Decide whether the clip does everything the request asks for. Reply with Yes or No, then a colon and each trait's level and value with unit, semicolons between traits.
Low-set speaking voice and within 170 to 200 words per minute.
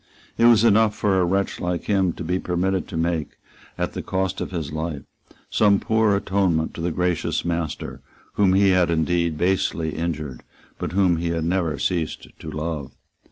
Yes: very low, 90 Hz; average, 180 wpm